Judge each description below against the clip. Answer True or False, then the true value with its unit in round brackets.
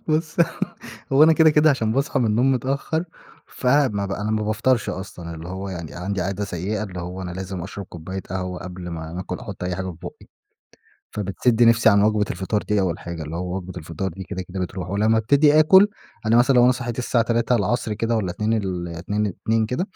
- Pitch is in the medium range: False (105 Hz)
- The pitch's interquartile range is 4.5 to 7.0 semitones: True (4.8 semitones)